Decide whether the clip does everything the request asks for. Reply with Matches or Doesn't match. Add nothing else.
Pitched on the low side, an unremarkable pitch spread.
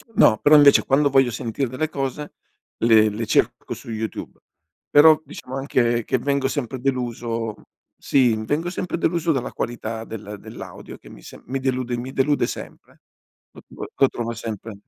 Matches